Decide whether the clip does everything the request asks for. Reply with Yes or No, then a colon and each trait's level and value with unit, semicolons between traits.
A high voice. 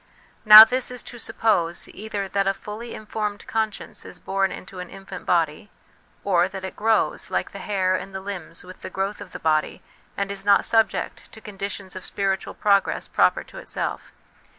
Yes: high, 195 Hz